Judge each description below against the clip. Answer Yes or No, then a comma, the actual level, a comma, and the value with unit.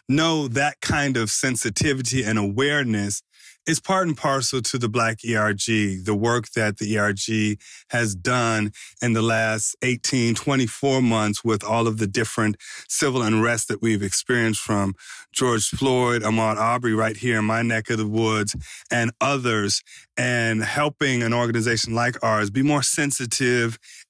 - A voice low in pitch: Yes, low, 115 Hz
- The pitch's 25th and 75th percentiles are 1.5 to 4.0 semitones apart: Yes, average, 2.8 semitones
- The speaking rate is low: No, average, 155 wpm